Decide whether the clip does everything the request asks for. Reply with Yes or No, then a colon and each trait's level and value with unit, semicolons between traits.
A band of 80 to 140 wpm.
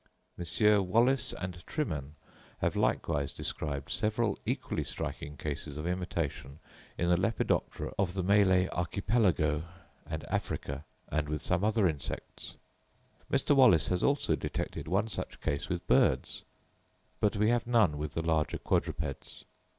Yes: slow, 135 wpm